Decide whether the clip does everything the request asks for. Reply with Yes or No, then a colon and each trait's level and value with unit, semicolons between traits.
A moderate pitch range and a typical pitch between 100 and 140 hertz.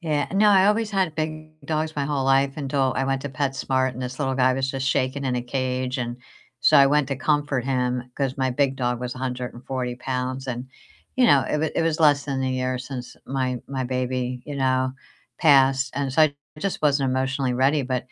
No: narrow, 2.1 semitones; low, 135 Hz